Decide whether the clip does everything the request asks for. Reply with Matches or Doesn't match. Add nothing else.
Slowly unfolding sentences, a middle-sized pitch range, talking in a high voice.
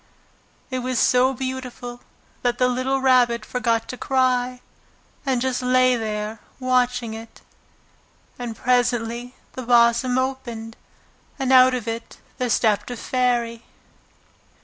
Doesn't match